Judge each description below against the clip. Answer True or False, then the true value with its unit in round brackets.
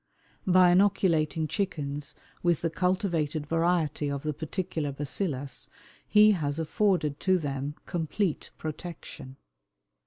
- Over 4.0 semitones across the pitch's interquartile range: False (3.6 semitones)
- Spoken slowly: True (105 wpm)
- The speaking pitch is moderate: True (160 Hz)